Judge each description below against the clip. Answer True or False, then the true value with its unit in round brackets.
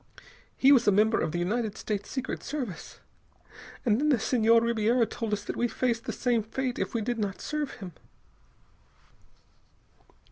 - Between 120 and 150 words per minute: False (170 wpm)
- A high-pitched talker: True (230 Hz)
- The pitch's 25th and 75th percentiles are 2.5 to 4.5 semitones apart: True (2.9 semitones)